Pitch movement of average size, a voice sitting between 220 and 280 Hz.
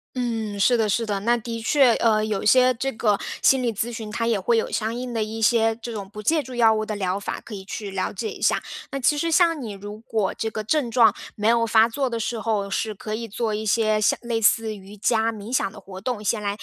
No: narrow, 2.0 semitones; high, 225 Hz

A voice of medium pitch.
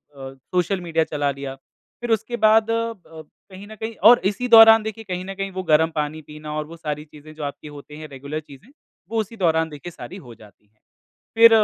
Yes: medium, 165 Hz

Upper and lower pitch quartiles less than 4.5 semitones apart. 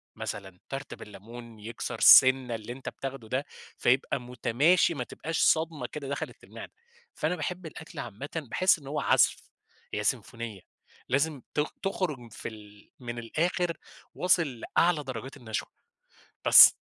No: average, 5.2 semitones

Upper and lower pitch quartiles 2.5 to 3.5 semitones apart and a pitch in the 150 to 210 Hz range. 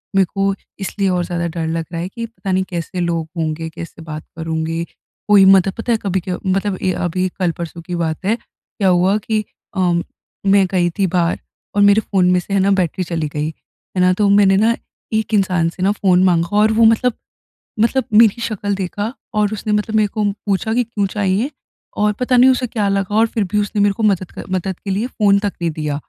Yes: average, 3.1 semitones; high, 195 Hz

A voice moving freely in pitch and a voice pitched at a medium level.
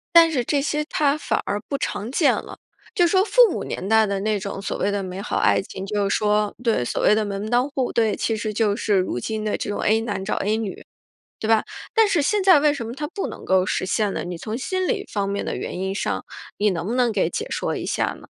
No: wide, 6.1 semitones; high, 220 Hz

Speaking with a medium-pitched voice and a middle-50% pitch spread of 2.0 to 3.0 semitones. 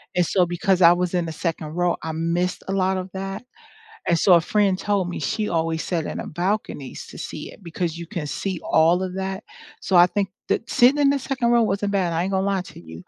Yes: medium, 180 Hz; average, 2.7 semitones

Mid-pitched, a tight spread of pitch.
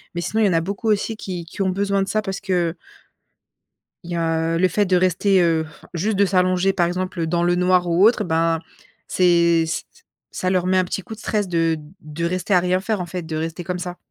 Yes: medium, 180 Hz; narrow, 2.3 semitones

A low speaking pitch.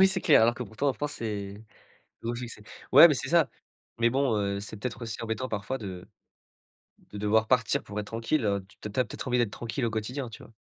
Yes: low, 115 Hz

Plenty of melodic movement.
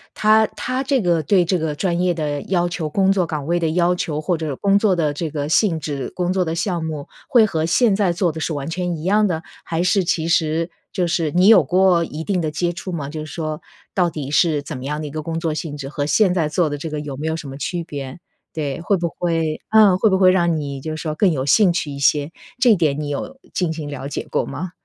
No: average, 3.2 semitones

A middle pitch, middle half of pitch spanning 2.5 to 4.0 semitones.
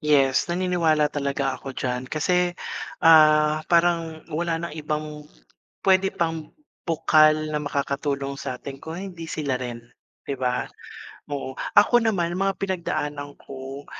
Yes: medium, 155 Hz; average, 3.3 semitones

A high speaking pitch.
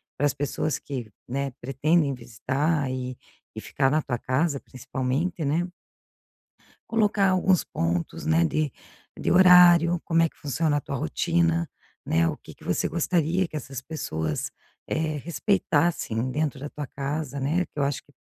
No: medium, 145 Hz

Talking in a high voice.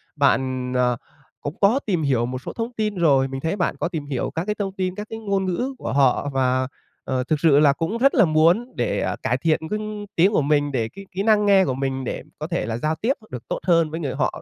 No: medium, 160 Hz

